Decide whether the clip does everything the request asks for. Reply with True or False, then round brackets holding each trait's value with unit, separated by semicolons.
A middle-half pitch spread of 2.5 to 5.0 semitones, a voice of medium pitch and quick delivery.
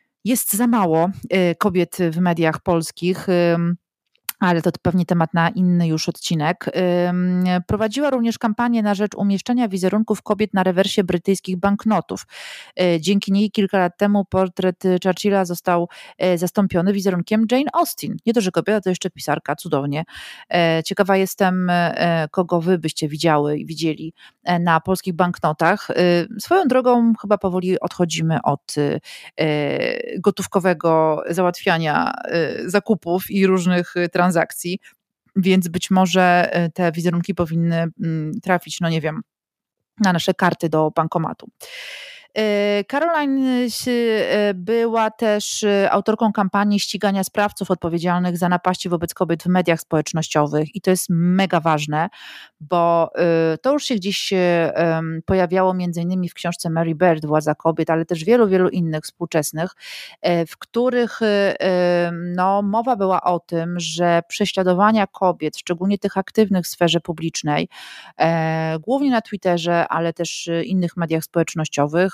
False (3.2 semitones; 180 Hz; 125 wpm)